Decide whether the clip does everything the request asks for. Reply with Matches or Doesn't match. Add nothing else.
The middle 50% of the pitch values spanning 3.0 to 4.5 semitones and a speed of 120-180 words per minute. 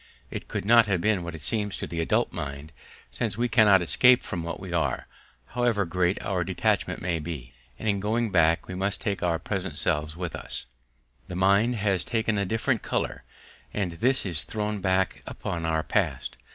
Doesn't match